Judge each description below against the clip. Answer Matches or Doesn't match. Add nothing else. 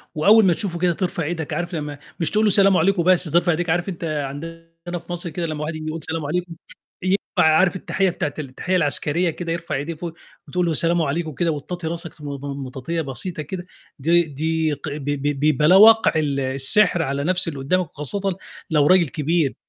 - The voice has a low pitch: Doesn't match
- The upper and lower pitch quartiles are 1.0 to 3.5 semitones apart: Matches